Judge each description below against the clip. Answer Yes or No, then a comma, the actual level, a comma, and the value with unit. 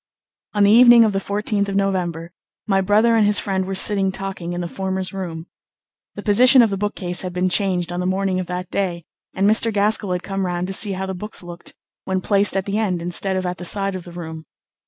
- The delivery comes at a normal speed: No, fast, 240 wpm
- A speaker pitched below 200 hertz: Yes, high, 190 Hz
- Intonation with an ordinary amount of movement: No, narrow, 2.2 semitones